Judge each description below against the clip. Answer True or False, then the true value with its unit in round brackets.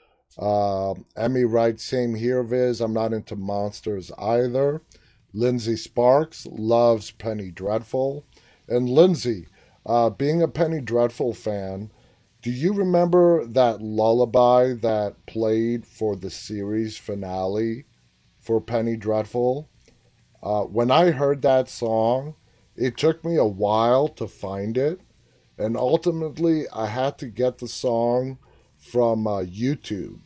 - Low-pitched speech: True (115 Hz)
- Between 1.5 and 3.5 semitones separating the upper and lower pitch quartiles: True (2.8 semitones)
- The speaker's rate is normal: False (125 wpm)